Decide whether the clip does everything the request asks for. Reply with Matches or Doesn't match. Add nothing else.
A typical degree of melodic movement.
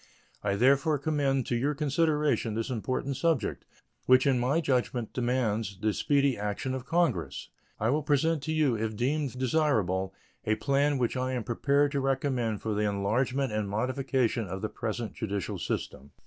Matches